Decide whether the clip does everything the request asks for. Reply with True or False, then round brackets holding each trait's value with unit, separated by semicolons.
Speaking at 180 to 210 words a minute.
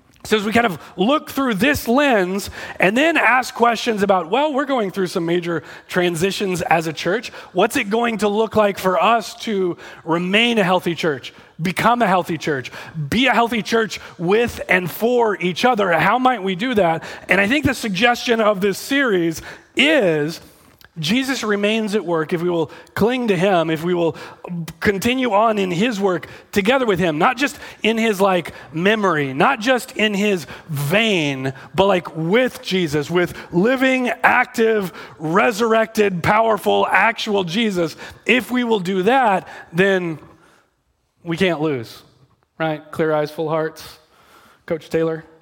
False (165 wpm)